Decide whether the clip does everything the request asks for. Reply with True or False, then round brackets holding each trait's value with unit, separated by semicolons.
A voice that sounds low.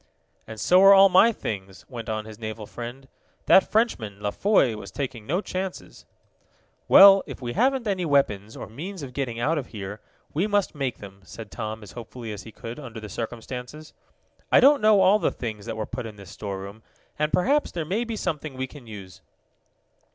True (125 Hz)